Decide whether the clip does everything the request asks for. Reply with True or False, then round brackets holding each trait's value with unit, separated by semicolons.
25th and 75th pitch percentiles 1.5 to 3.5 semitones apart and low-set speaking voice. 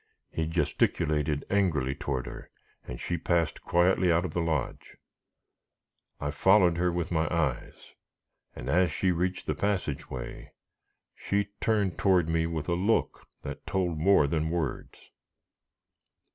True (3.1 semitones; 85 Hz)